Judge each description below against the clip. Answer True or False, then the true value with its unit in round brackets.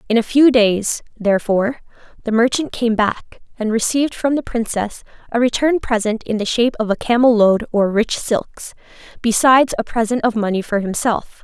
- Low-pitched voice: False (230 Hz)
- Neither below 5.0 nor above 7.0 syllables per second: True (5.2 syllables/s)